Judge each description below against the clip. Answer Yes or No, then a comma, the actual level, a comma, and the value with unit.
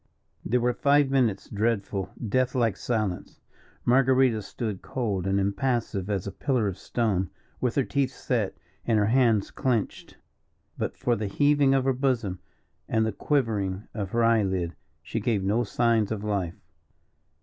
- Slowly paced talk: No, average, 155 wpm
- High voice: No, low, 115 Hz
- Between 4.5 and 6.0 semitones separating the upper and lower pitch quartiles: No, average, 4.1 semitones